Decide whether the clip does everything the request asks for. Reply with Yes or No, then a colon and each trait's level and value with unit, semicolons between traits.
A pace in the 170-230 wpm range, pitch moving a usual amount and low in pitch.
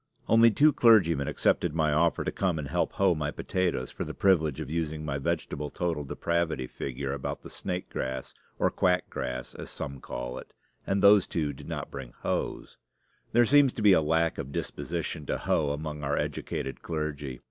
Yes: average, 190 wpm; average, 4.2 semitones; very low, 80 Hz